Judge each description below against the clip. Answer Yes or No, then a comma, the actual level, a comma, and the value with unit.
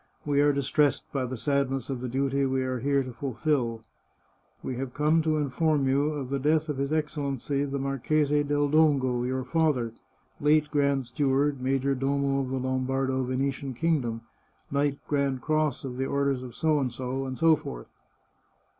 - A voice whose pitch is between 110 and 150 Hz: Yes, medium, 140 Hz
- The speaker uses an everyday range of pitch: No, narrow, 2.0 semitones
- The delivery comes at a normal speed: Yes, average, 170 wpm